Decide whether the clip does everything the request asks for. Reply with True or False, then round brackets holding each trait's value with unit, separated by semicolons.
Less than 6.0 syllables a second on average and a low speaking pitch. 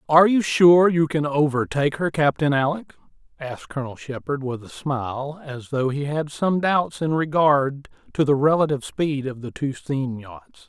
False (4.9 syllables/s; 145 Hz)